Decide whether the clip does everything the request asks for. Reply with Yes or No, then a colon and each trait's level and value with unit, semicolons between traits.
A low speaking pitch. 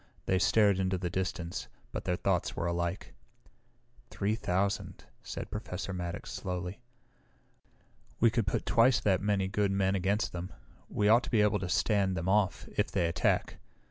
Yes: very low, 95 Hz